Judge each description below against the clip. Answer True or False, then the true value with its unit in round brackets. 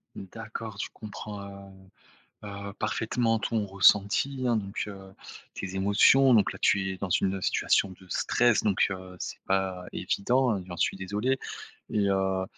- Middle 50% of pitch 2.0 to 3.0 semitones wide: True (2.4 semitones)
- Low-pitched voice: True (100 Hz)